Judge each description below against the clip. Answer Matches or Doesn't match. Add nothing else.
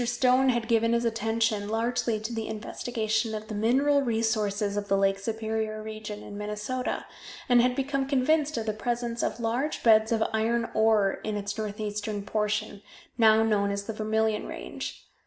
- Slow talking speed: Doesn't match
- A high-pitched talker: Matches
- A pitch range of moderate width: Doesn't match